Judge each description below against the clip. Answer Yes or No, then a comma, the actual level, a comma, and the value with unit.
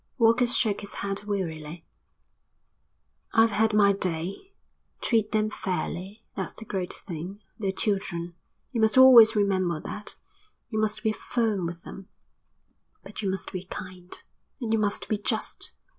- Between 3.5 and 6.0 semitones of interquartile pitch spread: No, average, 2.9 semitones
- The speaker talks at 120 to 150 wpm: Yes, average, 145 wpm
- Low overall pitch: No, high, 205 Hz